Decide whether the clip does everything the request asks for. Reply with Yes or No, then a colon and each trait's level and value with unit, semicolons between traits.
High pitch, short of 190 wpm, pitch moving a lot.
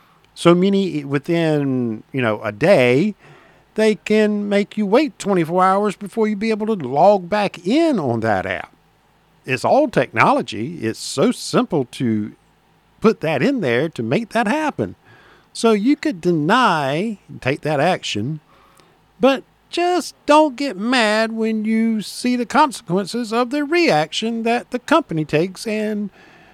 Yes: high, 210 Hz; average, 145 wpm; wide, 6.7 semitones